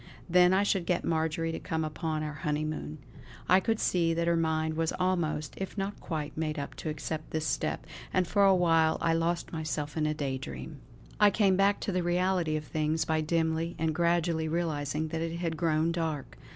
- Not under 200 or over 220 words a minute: Yes, fast, 205 wpm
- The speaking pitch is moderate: Yes, medium, 165 Hz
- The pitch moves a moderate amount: No, narrow, 2.0 semitones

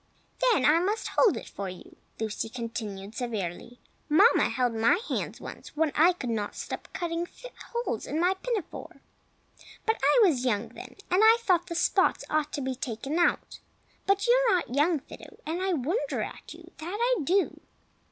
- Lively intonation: Yes, wide, 7.8 semitones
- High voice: Yes, very high, 315 Hz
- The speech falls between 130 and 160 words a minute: No, average, 180 wpm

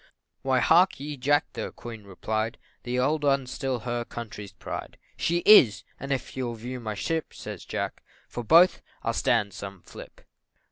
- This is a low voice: Yes, low, 125 Hz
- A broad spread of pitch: No, average, 4.4 semitones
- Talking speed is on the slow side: No, average, 170 wpm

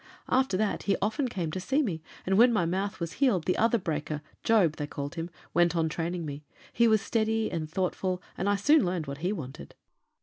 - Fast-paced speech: Yes, fast, 215 wpm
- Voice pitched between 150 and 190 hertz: Yes, medium, 185 Hz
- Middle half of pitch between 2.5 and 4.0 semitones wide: No, average, 5.0 semitones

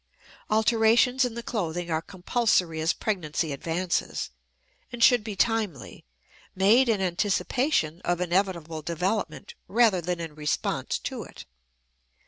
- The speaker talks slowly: Yes, slow, 120 wpm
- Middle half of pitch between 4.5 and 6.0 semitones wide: Yes, average, 5.1 semitones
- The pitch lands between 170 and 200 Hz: Yes, medium, 185 Hz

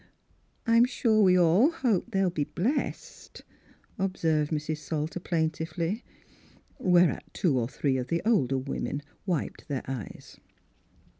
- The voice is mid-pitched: Yes, medium, 170 Hz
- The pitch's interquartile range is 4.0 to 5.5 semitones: Yes, average, 4.7 semitones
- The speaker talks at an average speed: No, slow, 130 wpm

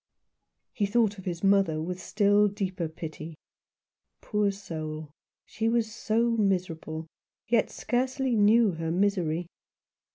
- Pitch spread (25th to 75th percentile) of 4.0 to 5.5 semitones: Yes, average, 4.7 semitones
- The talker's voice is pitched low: No, high, 200 Hz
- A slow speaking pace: Yes, slow, 120 wpm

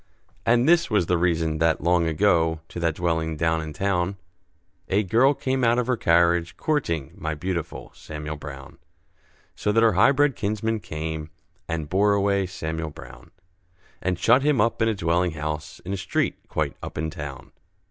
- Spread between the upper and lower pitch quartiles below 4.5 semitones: No, average, 4.9 semitones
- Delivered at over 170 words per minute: Yes, average, 180 wpm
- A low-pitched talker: Yes, very low, 85 Hz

